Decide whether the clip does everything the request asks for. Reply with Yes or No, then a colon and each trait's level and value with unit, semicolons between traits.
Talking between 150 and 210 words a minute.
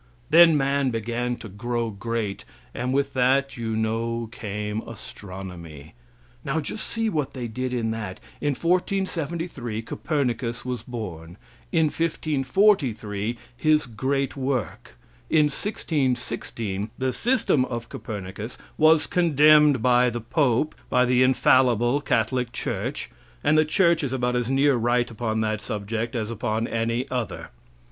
No: slow, 135 wpm